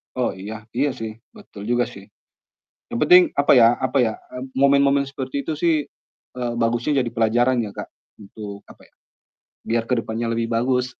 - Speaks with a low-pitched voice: Yes, low, 120 Hz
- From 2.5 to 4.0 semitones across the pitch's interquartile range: Yes, average, 2.8 semitones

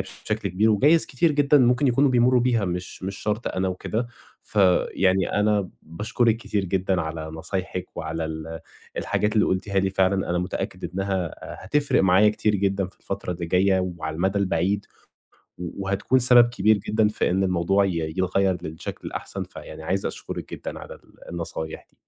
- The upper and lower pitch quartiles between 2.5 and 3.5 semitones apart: Yes, average, 3.1 semitones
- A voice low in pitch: Yes, very low, 95 Hz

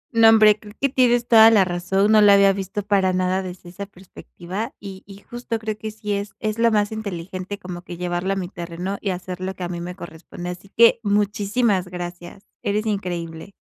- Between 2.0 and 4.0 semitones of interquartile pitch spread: Yes, average, 2.9 semitones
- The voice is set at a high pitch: Yes, high, 195 Hz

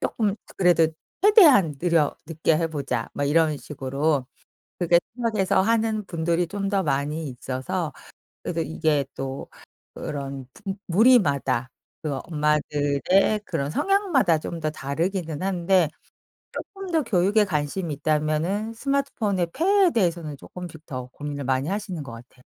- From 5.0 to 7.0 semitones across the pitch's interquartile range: Yes, average, 5.3 semitones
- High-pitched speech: No, medium, 165 Hz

